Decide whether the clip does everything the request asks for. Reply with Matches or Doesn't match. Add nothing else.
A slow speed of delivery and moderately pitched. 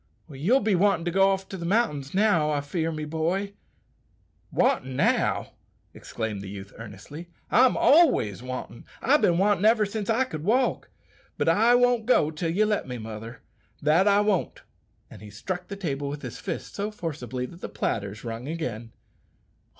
Doesn't match